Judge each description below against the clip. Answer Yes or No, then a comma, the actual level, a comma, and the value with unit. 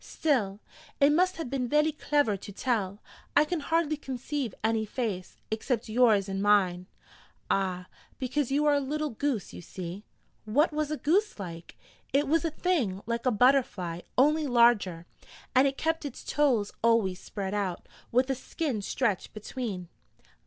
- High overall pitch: Yes, high, 245 Hz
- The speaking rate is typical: Yes, average, 160 wpm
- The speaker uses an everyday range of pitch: No, wide, 6.6 semitones